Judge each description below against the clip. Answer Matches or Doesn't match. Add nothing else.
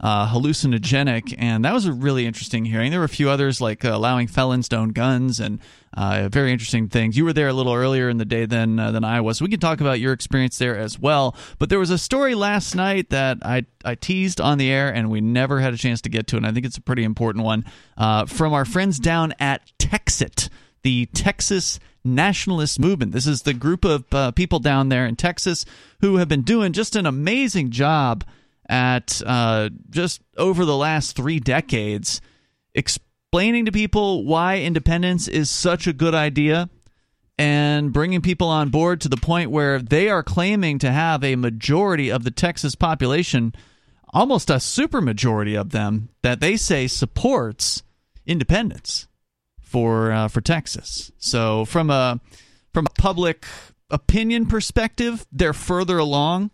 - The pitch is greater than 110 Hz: Matches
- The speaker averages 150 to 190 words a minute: Matches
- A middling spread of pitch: Doesn't match